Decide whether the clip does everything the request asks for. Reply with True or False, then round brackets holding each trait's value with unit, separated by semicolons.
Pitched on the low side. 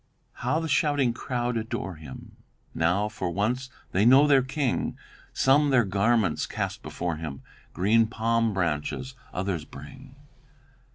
True (115 Hz)